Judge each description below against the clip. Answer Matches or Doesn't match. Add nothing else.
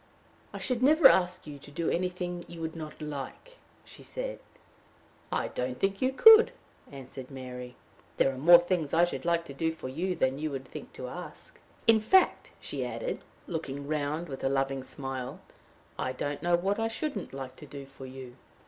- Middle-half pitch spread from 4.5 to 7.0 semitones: Matches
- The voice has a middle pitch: Matches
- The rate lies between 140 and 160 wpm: Doesn't match